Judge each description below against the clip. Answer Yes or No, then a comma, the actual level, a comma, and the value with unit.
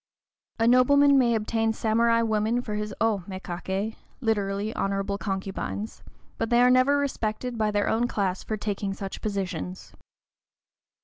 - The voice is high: Yes, high, 215 Hz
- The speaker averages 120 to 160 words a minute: Yes, average, 140 wpm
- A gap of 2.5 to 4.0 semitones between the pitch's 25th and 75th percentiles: Yes, average, 2.9 semitones